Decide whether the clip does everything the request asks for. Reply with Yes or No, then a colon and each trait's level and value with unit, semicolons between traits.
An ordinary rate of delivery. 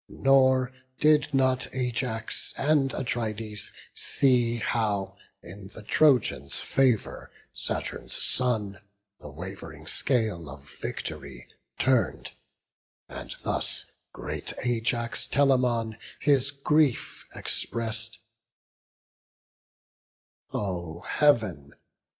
No: slow, 80 wpm